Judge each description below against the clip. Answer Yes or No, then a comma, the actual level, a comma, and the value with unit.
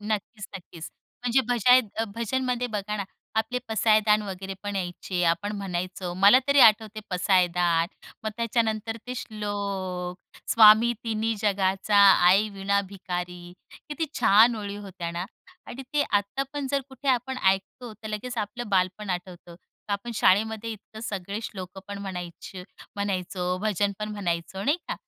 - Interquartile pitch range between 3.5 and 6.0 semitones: No, average, 3.0 semitones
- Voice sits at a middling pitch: No, high, 205 Hz